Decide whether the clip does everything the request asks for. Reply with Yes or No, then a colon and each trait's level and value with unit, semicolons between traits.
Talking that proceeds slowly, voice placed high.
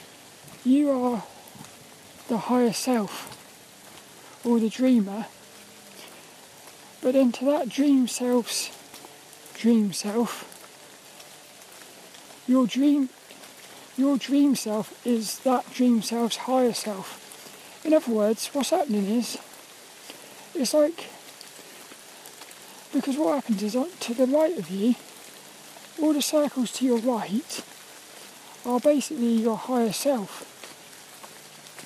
Yes: slow, 100 wpm; very high, 250 Hz